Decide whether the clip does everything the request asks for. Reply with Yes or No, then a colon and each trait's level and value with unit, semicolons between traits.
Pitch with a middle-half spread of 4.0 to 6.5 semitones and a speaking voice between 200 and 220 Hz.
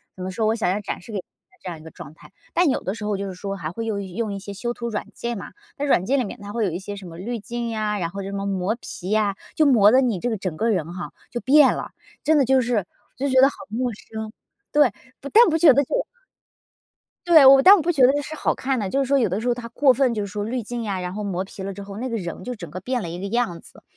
Yes: average, 4.8 semitones; high, 215 Hz